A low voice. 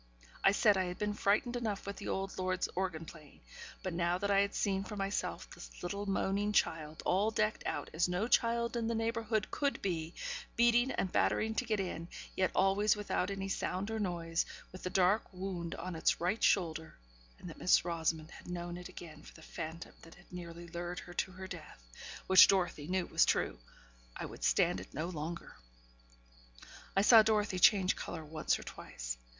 No: medium, 185 Hz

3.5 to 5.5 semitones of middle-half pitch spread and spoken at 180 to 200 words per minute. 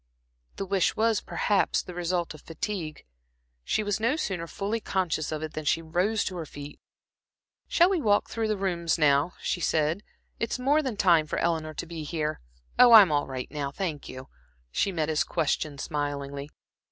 Yes: average, 5.0 semitones; average, 185 wpm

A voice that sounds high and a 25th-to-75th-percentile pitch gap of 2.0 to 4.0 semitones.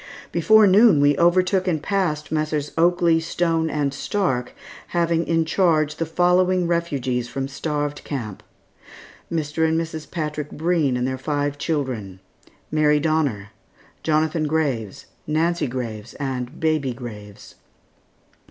No: medium, 155 Hz; average, 3.6 semitones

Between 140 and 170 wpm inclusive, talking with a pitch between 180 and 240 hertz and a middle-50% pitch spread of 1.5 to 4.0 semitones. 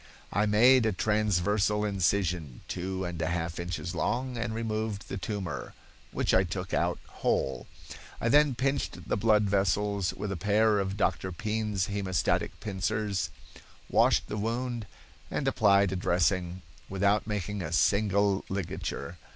No: average, 145 wpm; low, 100 Hz; narrow, 2.6 semitones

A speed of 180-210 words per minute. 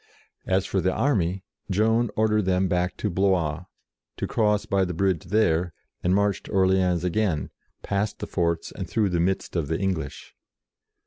No: average, 170 wpm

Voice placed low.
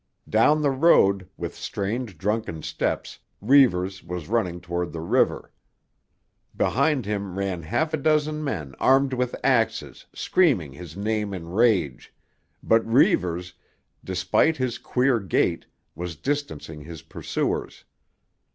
Yes: low, 100 Hz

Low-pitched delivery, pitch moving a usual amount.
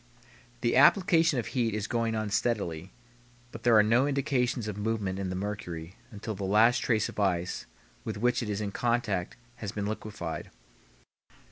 Yes: low, 110 Hz; average, 3.3 semitones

